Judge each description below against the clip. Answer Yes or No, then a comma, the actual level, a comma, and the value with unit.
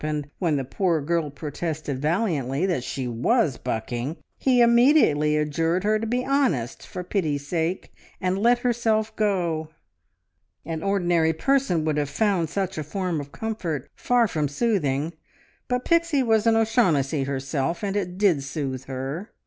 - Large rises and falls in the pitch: Yes, wide, 6.8 semitones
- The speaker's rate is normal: Yes, average, 150 wpm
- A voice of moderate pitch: Yes, medium, 170 Hz